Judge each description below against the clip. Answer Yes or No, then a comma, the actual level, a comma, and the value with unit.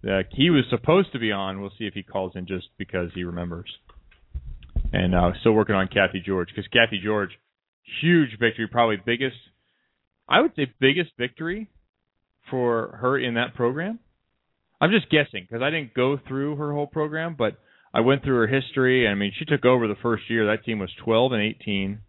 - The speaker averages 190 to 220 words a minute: Yes, average, 200 wpm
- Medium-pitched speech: No, low, 115 Hz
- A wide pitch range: Yes, wide, 5.7 semitones